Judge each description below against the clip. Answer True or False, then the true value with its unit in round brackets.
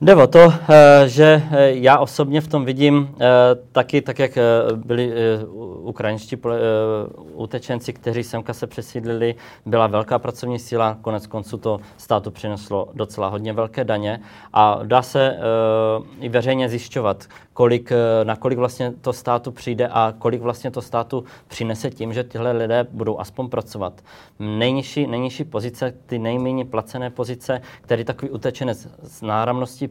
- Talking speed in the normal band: True (140 wpm)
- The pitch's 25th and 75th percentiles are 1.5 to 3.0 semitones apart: True (2.6 semitones)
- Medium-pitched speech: False (120 Hz)